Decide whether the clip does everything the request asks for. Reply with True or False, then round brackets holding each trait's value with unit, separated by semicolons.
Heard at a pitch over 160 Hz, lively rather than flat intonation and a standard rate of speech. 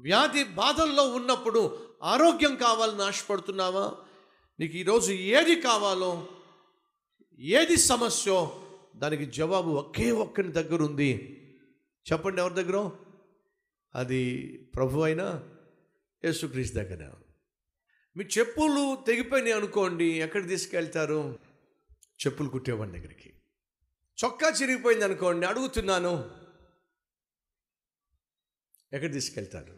True (190 Hz; 7.7 semitones; 80 wpm)